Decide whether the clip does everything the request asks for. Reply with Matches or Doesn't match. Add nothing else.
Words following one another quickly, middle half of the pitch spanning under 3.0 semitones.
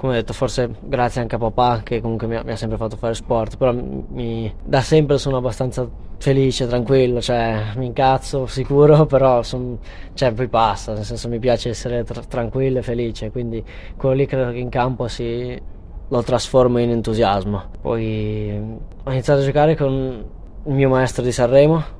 Matches